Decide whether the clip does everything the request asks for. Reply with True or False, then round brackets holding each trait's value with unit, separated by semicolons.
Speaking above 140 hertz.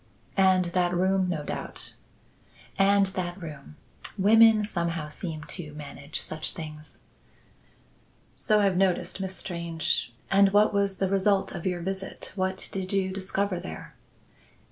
True (185 Hz)